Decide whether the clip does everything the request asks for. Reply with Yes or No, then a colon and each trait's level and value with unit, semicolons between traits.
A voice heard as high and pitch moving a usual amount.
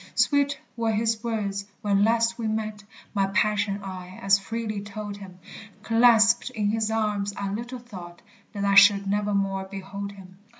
No: high, 205 Hz; narrow, 2.2 semitones